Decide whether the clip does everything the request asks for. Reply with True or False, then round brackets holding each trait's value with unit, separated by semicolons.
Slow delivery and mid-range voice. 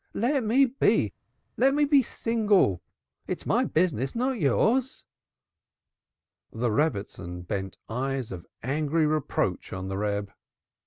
True (120 wpm; 150 Hz)